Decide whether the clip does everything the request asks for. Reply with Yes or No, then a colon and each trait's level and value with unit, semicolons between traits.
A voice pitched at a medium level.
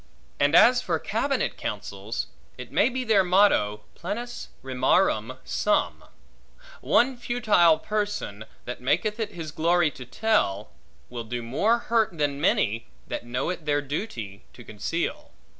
Yes: medium, 160 Hz